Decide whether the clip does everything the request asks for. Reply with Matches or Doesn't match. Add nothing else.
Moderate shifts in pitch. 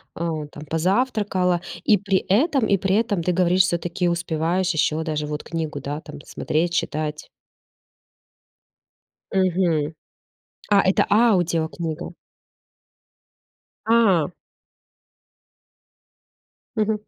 Matches